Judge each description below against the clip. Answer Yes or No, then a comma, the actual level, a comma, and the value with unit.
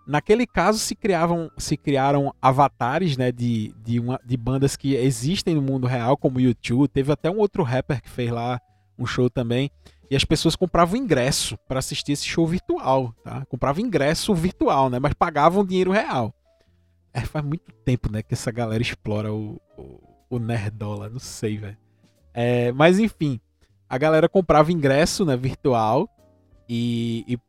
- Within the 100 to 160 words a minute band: No, average, 170 wpm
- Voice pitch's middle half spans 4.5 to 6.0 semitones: Yes, average, 4.9 semitones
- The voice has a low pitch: Yes, low, 130 Hz